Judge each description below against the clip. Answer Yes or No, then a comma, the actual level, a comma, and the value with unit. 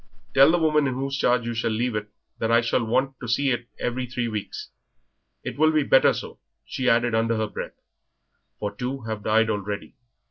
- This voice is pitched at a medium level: No, low, 120 Hz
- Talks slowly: No, average, 200 wpm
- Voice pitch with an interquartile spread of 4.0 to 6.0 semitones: No, average, 3.0 semitones